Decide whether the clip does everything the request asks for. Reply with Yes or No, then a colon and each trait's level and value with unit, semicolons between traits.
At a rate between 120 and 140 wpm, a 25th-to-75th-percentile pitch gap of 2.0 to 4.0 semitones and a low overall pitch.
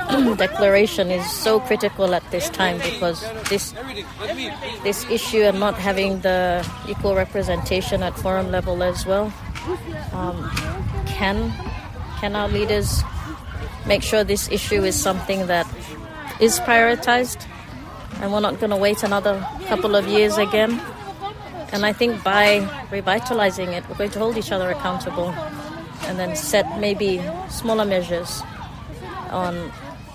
No: slow, 135 wpm; average, 2.7 semitones; high, 200 Hz